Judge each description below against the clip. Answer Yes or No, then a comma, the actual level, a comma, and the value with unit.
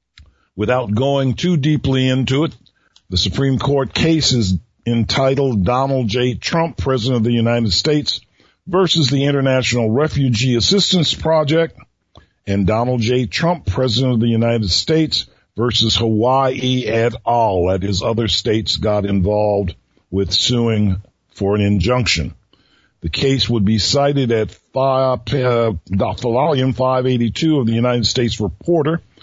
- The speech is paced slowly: Yes, slow, 130 wpm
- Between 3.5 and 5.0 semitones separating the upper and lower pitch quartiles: Yes, average, 4.1 semitones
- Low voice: Yes, low, 120 Hz